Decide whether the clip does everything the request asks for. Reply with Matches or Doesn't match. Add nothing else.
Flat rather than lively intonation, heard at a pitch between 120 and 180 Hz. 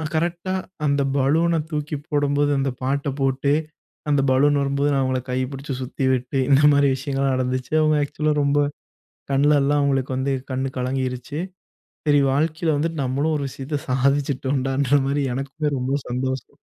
Matches